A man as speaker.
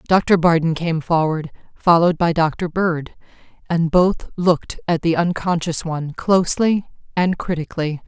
No: female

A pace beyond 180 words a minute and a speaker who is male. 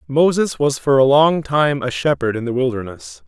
Yes: average, 200 wpm; male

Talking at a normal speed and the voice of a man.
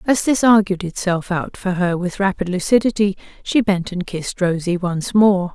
No: average, 185 wpm; female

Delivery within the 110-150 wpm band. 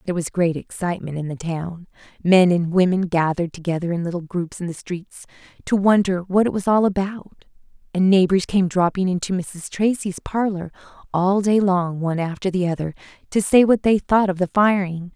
No: average, 190 wpm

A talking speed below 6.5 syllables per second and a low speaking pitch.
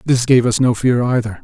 Yes: 5.3 syllables/s; low, 120 Hz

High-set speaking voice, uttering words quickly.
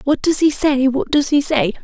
Yes: very high, 280 Hz; fast, 260 wpm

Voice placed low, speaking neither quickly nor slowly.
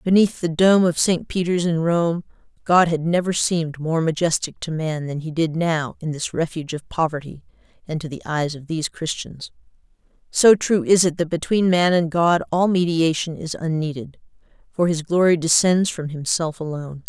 No: medium, 165 Hz; average, 180 wpm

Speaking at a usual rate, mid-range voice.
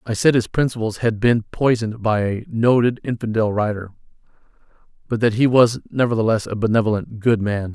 No: average, 165 wpm; low, 115 Hz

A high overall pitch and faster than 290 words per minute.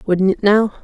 No: high, 200 Hz; fast, 215 wpm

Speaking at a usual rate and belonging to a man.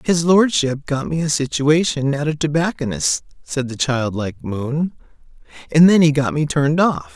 Yes: average, 175 wpm; male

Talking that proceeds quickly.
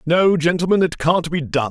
Yes: fast, 210 wpm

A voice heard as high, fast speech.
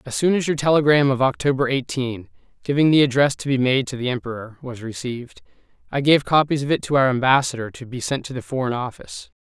No: low, 130 Hz; fast, 215 wpm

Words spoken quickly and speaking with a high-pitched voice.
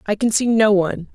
Yes: fast, 265 wpm; high, 210 Hz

